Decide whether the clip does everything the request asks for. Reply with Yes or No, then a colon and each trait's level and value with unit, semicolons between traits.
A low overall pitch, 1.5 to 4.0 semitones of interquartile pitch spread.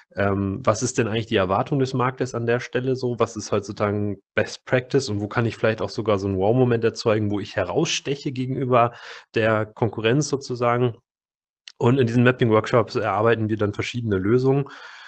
Yes: low, 115 Hz; average, 2.9 semitones